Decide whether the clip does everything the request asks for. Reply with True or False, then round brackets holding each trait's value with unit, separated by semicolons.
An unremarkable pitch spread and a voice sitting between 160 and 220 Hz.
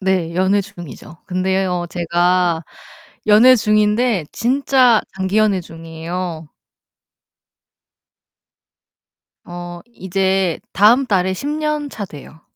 True (3.5 semitones; 190 Hz)